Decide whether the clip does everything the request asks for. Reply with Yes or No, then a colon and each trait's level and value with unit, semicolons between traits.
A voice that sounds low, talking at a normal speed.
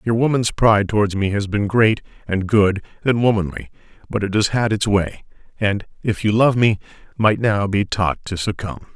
Yes: low, 105 Hz; average, 195 wpm